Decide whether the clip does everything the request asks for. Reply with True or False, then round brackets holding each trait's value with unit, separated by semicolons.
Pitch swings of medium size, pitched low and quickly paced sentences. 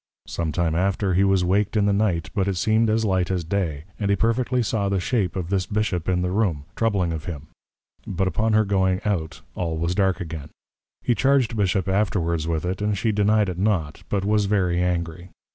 True (3.3 semitones; 95 Hz; 210 wpm)